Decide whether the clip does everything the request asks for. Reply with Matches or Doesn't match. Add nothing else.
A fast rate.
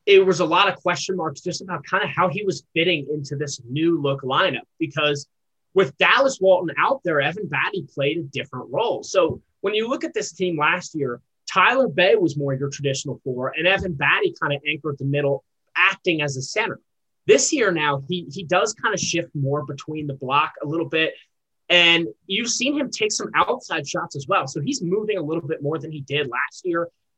Matches